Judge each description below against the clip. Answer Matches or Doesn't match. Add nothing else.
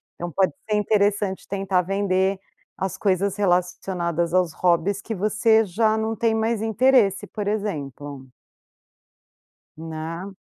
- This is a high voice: Matches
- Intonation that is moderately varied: Matches